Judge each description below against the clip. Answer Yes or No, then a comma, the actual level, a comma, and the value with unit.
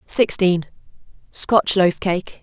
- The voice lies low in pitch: No, medium, 185 Hz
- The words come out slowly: Yes, slow, 75 wpm